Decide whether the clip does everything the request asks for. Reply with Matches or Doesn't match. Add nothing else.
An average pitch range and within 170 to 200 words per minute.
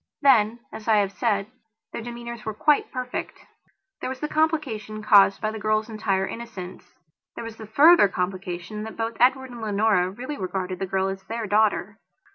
Matches